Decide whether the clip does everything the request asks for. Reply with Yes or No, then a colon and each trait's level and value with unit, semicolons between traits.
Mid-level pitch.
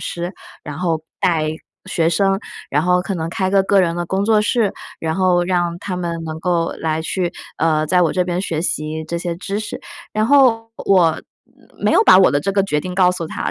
Yes: medium, 175 Hz